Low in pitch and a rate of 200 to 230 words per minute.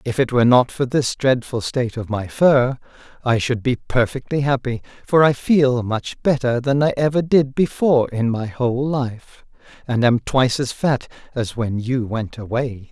No: low, 125 Hz; average, 185 wpm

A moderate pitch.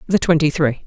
Yes: medium, 155 Hz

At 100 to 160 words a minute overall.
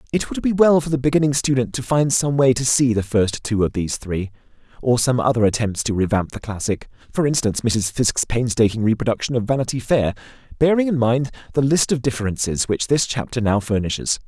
No: fast, 205 wpm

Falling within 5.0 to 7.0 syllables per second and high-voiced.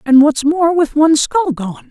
No: 4.5 syllables/s; very high, 295 Hz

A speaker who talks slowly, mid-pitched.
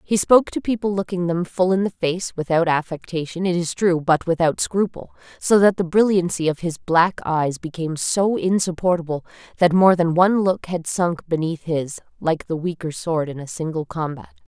No: average, 190 wpm; medium, 170 Hz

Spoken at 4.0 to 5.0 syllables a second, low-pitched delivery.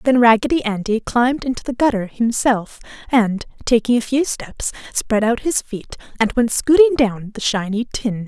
No: 4.8 syllables/s; high, 235 Hz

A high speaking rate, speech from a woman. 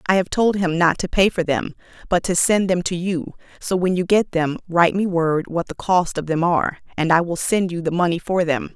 Yes: fast, 260 wpm; female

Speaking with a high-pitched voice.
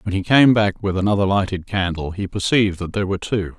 No: very low, 95 Hz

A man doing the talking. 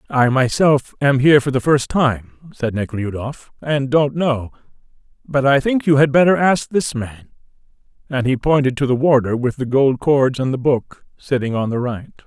Yes: male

